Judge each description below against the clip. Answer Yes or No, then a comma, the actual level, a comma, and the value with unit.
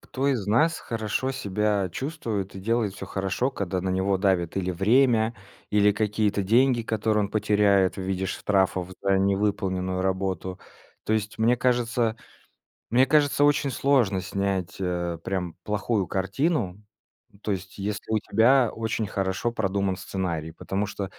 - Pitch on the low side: Yes, low, 100 Hz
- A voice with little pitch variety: No, average, 3.1 semitones